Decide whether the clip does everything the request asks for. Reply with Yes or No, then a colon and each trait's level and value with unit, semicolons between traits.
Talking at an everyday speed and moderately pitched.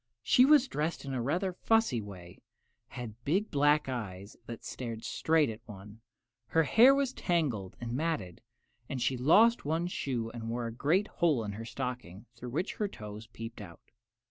No: average, 185 wpm; low, 125 Hz